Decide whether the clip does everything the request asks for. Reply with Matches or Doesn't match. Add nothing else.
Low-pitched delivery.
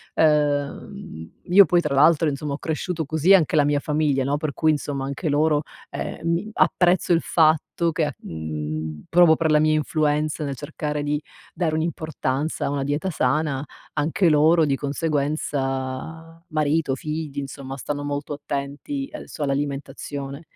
Doesn't match